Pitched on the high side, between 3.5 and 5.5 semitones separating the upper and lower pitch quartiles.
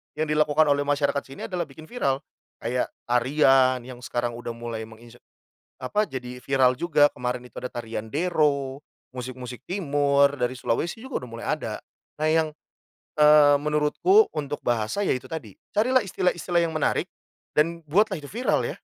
No: medium, 140 Hz; average, 4.0 semitones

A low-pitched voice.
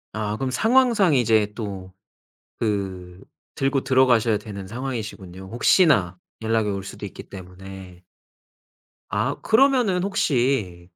Yes: low, 110 Hz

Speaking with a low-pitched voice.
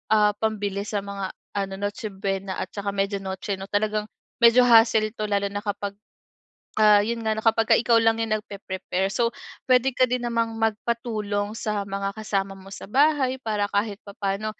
No: high, 210 Hz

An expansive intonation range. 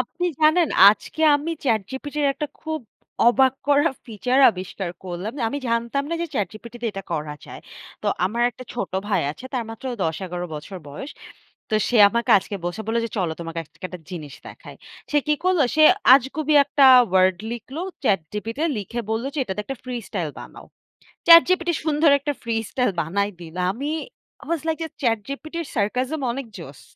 Yes: wide, 6.9 semitones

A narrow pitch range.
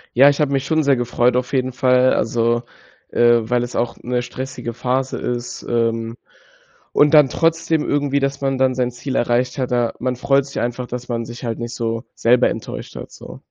Yes: narrow, 2.2 semitones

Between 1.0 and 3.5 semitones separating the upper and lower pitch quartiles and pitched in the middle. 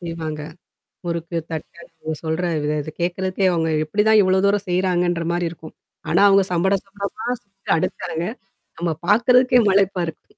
Yes: average, 3.1 semitones; medium, 180 Hz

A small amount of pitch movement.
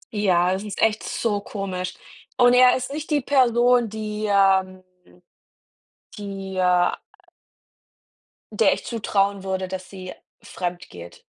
No: average, 3.5 semitones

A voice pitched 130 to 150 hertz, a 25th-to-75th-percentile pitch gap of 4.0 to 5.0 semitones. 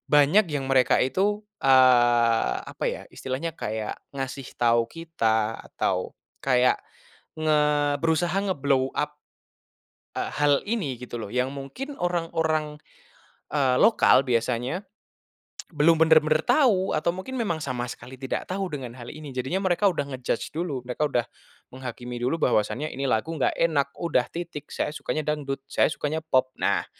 Yes: medium, 140 Hz; average, 4.6 semitones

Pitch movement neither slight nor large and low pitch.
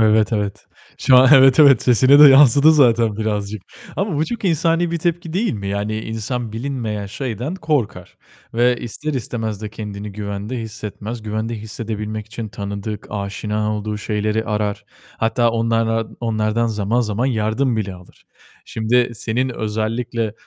Yes: average, 3.0 semitones; low, 110 Hz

